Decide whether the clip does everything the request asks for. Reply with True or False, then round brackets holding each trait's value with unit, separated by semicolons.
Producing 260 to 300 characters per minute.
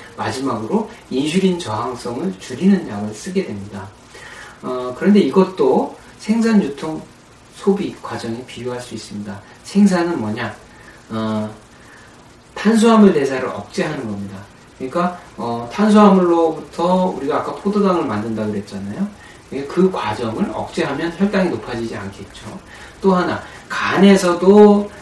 True (290 characters per minute)